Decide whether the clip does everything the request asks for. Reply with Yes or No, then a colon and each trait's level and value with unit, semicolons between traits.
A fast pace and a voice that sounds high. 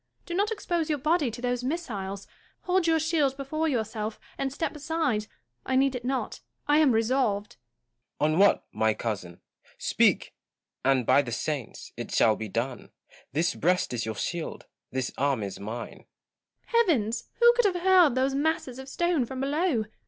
No: average, 175 wpm; very high, 255 Hz